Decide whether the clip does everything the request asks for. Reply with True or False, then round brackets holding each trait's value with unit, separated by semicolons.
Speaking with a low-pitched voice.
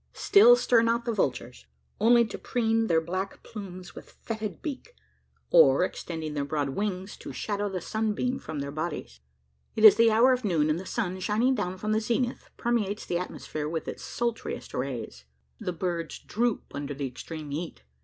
False (200 Hz)